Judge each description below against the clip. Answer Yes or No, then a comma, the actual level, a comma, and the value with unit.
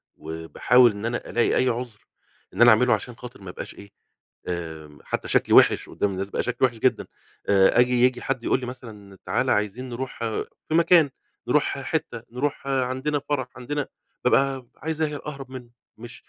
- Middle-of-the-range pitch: No, low, 125 Hz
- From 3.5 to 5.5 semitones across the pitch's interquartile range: Yes, average, 4.1 semitones